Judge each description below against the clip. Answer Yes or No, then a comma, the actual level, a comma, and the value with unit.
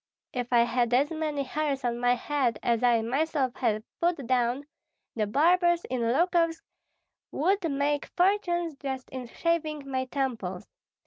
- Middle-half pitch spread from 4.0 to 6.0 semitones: Yes, average, 4.8 semitones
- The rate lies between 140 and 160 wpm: Yes, average, 145 wpm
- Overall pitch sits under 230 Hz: No, very high, 275 Hz